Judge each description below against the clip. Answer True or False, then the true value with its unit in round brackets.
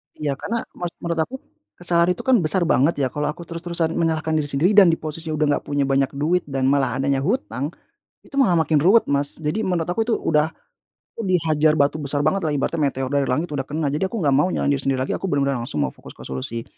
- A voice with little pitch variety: False (3.6 semitones)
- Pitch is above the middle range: False (155 Hz)